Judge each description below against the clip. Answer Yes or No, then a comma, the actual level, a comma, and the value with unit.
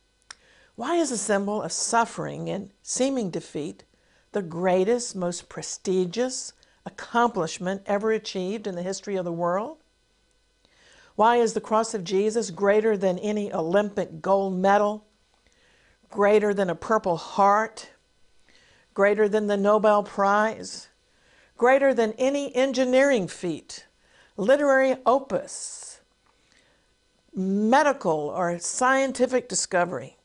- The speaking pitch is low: No, high, 210 Hz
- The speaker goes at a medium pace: No, slow, 110 wpm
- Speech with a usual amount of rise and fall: Yes, average, 3.9 semitones